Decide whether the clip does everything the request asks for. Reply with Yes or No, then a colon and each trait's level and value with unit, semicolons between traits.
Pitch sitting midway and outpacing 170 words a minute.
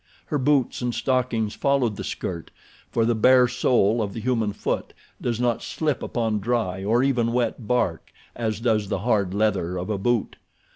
No: low, 115 Hz; average, 180 wpm